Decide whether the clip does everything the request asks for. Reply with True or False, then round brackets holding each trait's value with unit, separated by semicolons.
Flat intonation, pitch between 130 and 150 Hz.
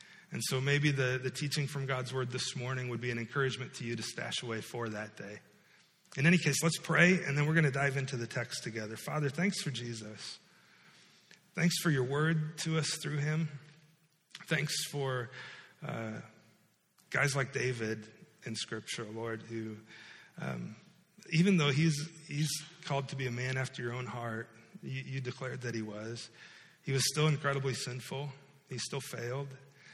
False (4.3 semitones; 135 Hz)